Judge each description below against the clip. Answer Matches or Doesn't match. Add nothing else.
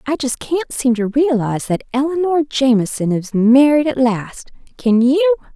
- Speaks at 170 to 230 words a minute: Doesn't match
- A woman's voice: Matches